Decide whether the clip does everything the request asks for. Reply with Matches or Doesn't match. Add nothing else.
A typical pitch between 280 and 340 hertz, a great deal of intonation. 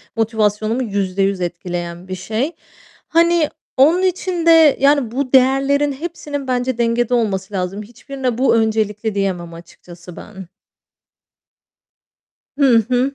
Doesn't match